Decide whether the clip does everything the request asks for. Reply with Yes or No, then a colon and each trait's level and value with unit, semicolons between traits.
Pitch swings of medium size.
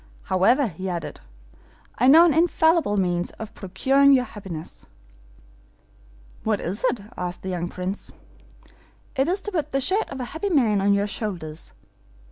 No: wide, 7.1 semitones